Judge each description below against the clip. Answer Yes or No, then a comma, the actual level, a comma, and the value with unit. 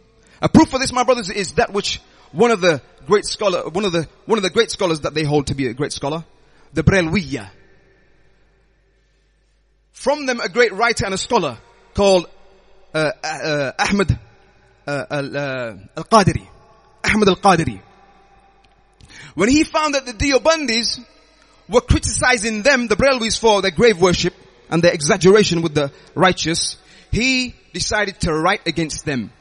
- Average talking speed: Yes, average, 155 wpm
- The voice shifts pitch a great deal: Yes, wide, 6.7 semitones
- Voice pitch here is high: Yes, high, 195 Hz